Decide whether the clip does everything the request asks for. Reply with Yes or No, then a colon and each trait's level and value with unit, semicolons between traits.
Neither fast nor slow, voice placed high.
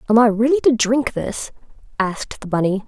Yes: average, 190 wpm; high, 230 Hz